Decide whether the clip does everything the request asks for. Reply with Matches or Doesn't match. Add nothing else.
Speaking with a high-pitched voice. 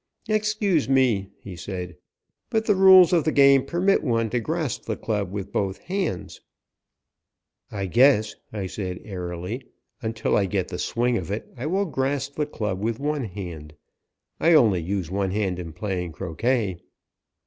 Doesn't match